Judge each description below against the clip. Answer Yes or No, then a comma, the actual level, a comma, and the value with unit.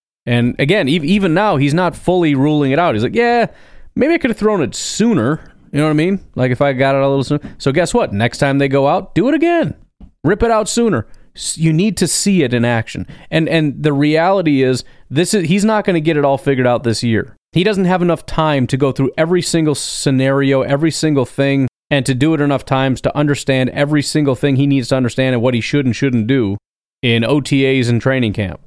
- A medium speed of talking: No, fast, 240 wpm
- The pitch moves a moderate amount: Yes, average, 4.3 semitones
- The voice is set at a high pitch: No, medium, 145 Hz